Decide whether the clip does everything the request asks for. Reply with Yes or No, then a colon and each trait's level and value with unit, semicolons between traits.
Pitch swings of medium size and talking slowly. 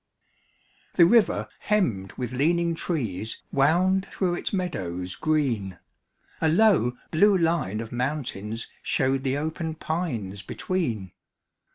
No: wide, 7.5 semitones; slow, 110 wpm